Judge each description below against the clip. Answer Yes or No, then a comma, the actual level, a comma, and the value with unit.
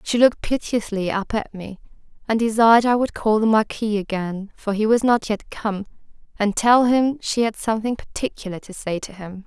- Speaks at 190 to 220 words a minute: Yes, average, 195 wpm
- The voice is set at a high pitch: Yes, high, 215 Hz